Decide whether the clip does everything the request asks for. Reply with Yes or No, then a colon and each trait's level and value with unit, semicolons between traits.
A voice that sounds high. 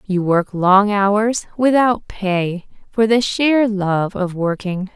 Yes: high, 200 Hz